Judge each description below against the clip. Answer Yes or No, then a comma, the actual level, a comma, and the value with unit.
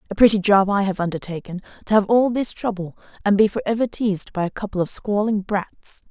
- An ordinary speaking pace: No, fast, 215 wpm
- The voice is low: No, high, 205 Hz